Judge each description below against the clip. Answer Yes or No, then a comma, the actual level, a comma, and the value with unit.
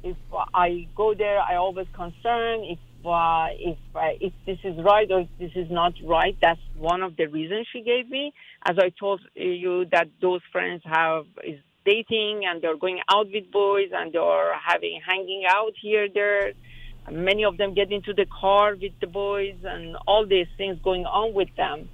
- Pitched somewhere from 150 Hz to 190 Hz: Yes, medium, 185 Hz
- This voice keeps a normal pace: Yes, average, 195 wpm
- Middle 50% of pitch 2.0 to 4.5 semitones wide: Yes, average, 3.3 semitones